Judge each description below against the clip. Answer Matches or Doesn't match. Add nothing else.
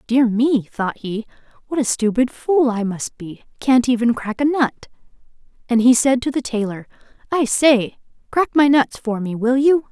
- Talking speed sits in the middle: Matches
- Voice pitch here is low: Doesn't match